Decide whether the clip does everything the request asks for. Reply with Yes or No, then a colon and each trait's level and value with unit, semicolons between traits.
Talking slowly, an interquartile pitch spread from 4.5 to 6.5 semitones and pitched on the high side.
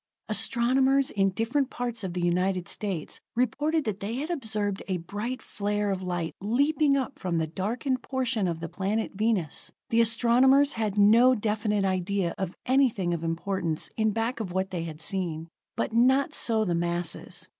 No: average, 170 wpm; average, 5.1 semitones; high, 210 Hz